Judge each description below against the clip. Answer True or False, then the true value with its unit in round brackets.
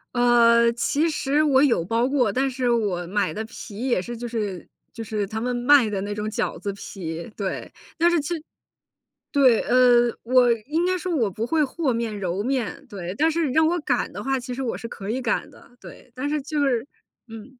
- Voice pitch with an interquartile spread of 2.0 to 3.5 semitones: False (4.2 semitones)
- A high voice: True (240 Hz)